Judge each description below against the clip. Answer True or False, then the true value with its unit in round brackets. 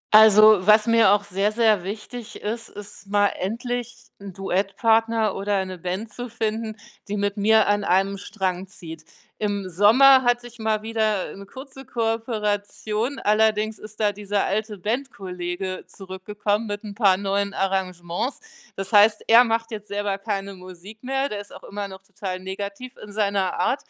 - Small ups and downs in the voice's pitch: True (2.3 semitones)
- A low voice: False (205 Hz)